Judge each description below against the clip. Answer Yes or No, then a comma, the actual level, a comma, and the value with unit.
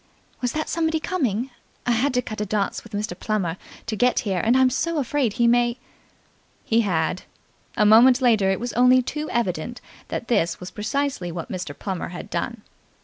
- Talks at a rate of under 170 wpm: No, average, 195 wpm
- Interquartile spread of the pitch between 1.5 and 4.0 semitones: No, average, 4.4 semitones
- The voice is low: No, high, 230 Hz